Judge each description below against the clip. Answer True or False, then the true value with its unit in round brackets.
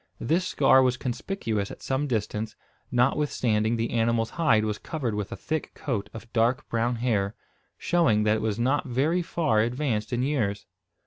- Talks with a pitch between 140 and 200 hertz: False (120 Hz)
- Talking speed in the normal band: True (170 wpm)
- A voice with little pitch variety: False (4.0 semitones)